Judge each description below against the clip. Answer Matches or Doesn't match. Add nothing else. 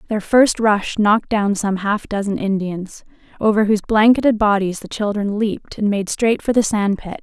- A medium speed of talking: Matches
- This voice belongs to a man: Doesn't match